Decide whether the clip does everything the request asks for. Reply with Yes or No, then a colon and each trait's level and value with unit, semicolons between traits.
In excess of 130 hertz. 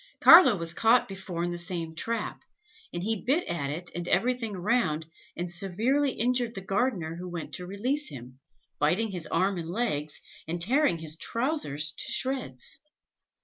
Yes: medium, 185 Hz